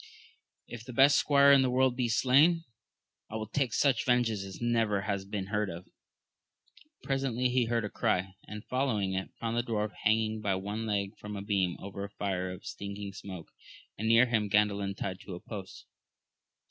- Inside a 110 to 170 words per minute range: No, average, 190 wpm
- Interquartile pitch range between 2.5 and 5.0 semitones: Yes, average, 3.5 semitones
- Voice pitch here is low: Yes, low, 105 Hz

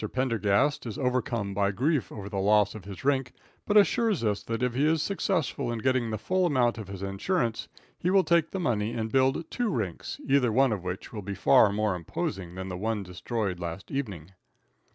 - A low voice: Yes, low, 115 Hz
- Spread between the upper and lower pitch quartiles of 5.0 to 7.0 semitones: Yes, wide, 5.4 semitones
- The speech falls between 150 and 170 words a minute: No, fast, 205 wpm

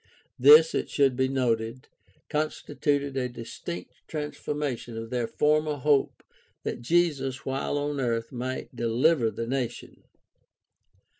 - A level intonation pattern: No, average, 3.6 semitones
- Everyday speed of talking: No, slow, 125 wpm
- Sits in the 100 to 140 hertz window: Yes, low, 135 Hz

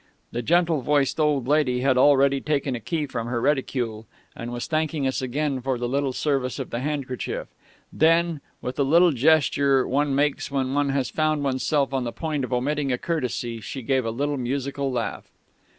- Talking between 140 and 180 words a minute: No, average, 190 wpm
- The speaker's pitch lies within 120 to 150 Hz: Yes, low, 135 Hz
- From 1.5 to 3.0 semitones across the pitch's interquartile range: Yes, narrow, 2.6 semitones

